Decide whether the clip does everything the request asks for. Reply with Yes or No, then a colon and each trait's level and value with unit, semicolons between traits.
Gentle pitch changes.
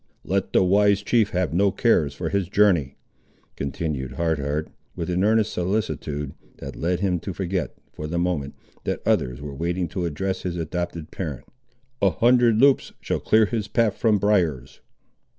No: average, 4.4 semitones